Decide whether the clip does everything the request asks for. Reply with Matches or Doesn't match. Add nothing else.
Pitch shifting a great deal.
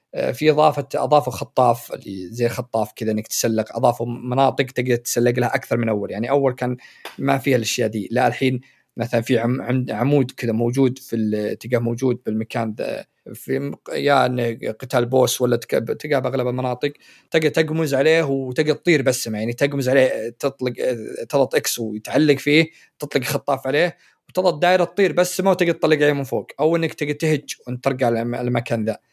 Doesn't match